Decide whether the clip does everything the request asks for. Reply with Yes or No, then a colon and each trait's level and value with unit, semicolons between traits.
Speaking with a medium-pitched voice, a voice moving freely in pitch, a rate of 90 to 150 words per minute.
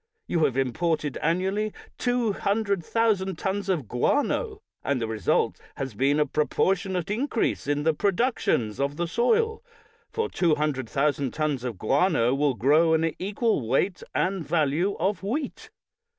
Yes: medium, 165 Hz; wide, 6.4 semitones; average, 140 wpm